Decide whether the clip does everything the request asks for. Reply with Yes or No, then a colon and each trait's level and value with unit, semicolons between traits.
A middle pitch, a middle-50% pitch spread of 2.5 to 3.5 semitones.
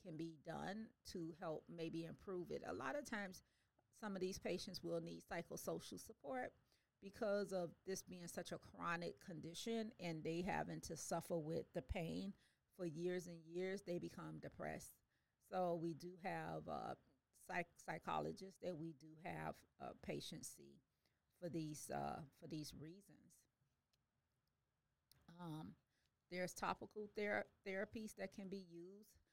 Yes: medium, 175 Hz; average, 2.8 semitones